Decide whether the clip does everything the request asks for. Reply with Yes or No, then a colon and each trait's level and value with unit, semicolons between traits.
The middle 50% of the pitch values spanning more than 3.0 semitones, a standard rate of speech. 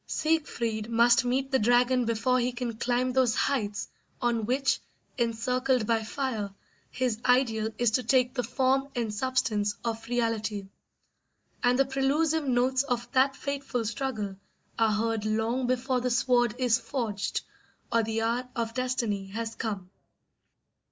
No: narrow, 2.4 semitones; average, 145 wpm